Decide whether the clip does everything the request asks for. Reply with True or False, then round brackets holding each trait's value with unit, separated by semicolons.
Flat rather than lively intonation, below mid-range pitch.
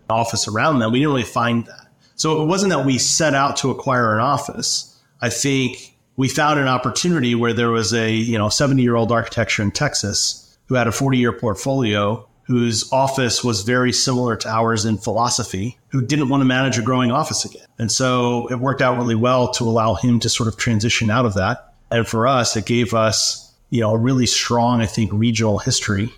True (2.3 semitones; 120 Hz)